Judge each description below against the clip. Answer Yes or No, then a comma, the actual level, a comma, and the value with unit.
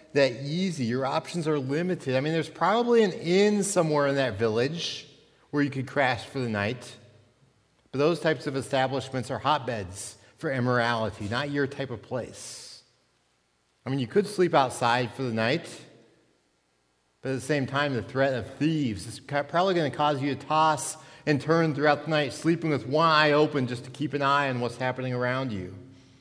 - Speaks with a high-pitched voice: No, low, 135 Hz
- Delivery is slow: No, average, 190 wpm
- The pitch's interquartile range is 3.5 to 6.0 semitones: Yes, average, 3.9 semitones